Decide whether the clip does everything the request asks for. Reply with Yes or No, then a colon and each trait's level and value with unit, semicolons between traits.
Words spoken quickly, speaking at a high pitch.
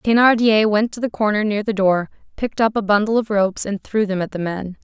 Yes: fast, 250 wpm; high, 210 Hz